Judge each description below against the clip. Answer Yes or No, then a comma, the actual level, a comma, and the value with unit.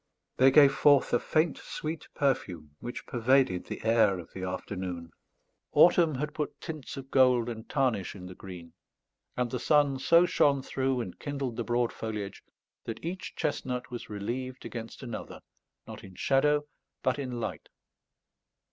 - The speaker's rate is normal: Yes, average, 155 wpm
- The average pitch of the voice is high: No, low, 125 Hz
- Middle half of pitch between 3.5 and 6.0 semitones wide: Yes, average, 4.1 semitones